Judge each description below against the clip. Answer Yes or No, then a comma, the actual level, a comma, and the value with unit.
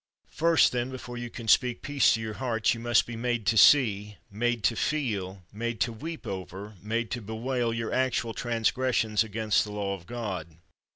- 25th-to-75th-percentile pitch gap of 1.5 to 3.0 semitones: Yes, narrow, 2.6 semitones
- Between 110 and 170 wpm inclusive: No, average, 185 wpm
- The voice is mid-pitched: No, low, 115 Hz